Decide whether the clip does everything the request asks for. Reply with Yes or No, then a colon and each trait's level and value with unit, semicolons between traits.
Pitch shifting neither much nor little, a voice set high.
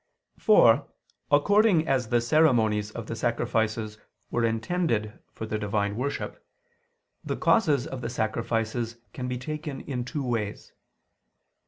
No: average, 4.2 semitones; low, 120 Hz